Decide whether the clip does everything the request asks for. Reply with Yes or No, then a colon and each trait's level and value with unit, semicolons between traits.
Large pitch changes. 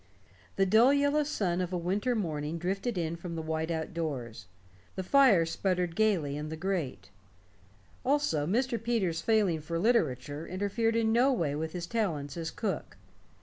Yes: wide, 5.8 semitones